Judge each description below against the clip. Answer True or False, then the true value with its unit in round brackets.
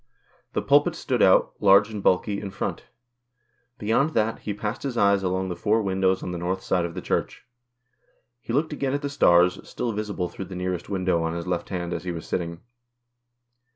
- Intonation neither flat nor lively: True (3.1 semitones)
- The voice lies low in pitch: True (95 Hz)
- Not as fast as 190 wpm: False (200 wpm)